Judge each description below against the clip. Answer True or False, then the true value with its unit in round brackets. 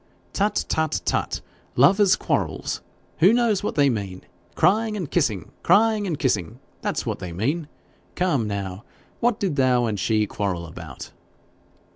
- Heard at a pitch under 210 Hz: True (140 Hz)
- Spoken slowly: False (150 wpm)